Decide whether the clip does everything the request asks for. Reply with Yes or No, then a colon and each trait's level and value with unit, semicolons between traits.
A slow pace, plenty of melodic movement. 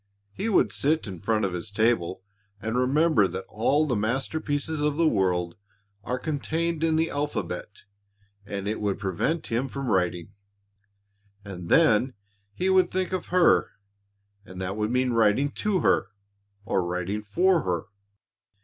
No: average, 150 wpm; wide, 8.2 semitones